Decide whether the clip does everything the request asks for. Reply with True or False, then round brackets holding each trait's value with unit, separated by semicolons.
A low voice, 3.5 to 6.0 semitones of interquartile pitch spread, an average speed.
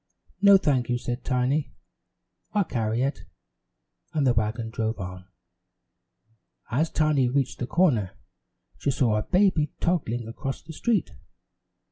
False (130 Hz; 5.1 semitones; 130 wpm)